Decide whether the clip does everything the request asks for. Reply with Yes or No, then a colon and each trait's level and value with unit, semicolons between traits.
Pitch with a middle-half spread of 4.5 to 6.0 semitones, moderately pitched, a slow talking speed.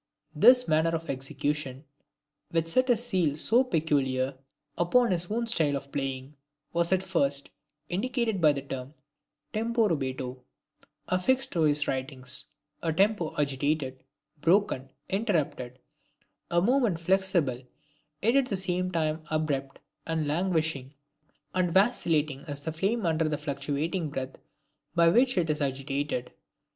Yes: average, 5.3 semitones; medium, 160 Hz; slow, 130 wpm